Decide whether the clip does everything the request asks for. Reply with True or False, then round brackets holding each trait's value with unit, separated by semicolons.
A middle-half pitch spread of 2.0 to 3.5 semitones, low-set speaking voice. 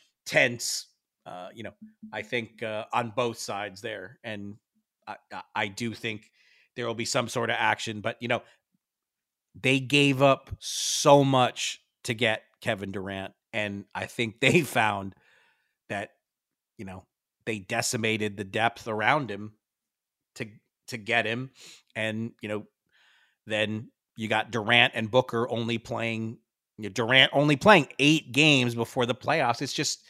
True (2.9 semitones; 115 Hz)